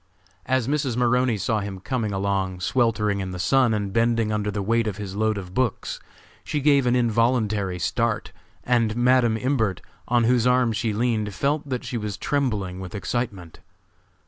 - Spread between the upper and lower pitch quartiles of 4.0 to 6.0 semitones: No, average, 3.6 semitones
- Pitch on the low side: Yes, low, 115 Hz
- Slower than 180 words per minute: Yes, average, 170 wpm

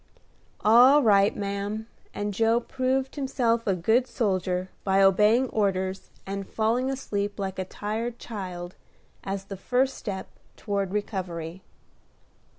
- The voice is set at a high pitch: Yes, high, 205 Hz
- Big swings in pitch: No, average, 3.4 semitones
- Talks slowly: Yes, slow, 125 wpm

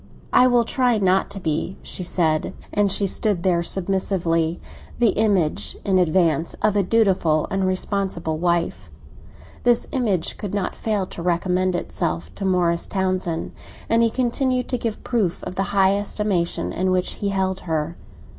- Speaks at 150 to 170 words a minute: Yes, average, 160 wpm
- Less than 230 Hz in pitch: Yes, high, 190 Hz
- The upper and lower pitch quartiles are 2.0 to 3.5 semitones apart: Yes, average, 3.2 semitones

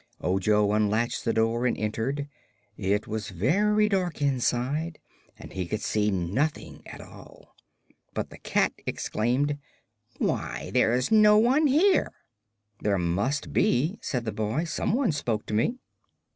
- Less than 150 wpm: Yes, average, 140 wpm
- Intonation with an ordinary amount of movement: No, wide, 7.2 semitones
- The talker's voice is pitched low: Yes, low, 120 Hz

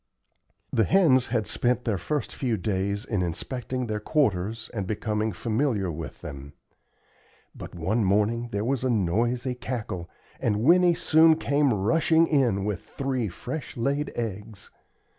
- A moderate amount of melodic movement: Yes, average, 4.6 semitones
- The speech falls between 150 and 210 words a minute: No, average, 140 wpm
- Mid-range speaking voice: No, low, 115 Hz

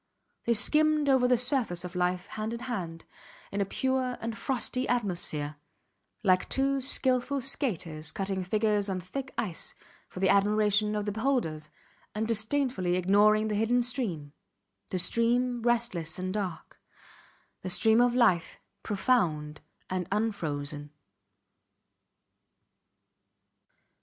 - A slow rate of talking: Yes, slow, 120 wpm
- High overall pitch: Yes, high, 210 Hz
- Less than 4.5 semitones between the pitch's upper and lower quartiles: No, average, 5.3 semitones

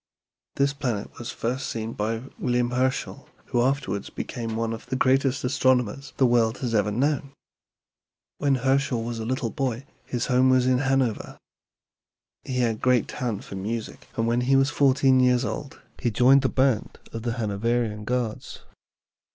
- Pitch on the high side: No, low, 125 Hz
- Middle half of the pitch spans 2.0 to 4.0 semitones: Yes, narrow, 2.6 semitones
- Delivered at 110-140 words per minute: No, average, 165 wpm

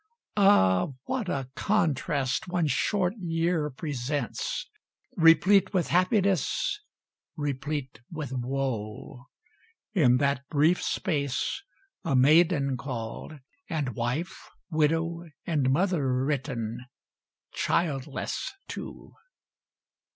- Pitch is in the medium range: Yes, medium, 150 Hz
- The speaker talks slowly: Yes, slow, 85 wpm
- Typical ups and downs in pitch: Yes, average, 4.8 semitones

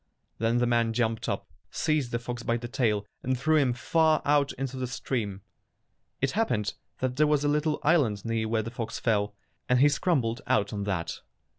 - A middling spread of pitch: Yes, average, 4.1 semitones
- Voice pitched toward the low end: Yes, low, 120 Hz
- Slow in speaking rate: No, average, 195 wpm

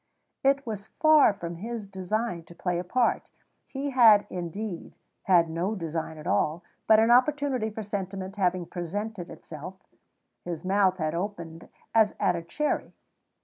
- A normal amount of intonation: Yes, average, 4.4 semitones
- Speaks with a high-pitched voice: Yes, high, 195 Hz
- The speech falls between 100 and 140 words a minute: No, average, 150 wpm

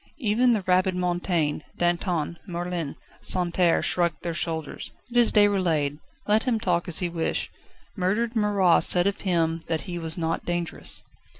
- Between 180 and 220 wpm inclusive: No, average, 155 wpm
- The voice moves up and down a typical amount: Yes, average, 3.0 semitones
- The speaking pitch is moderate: Yes, medium, 175 Hz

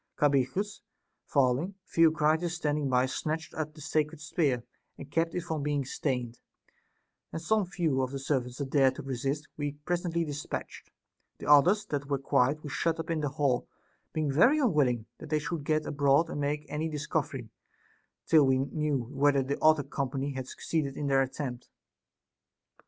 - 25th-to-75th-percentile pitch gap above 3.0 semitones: No, average, 2.7 semitones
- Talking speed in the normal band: Yes, average, 170 wpm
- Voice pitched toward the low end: No, medium, 145 Hz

